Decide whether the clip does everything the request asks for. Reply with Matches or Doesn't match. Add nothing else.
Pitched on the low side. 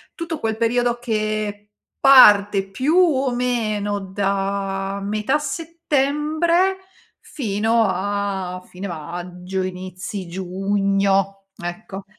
Doesn't match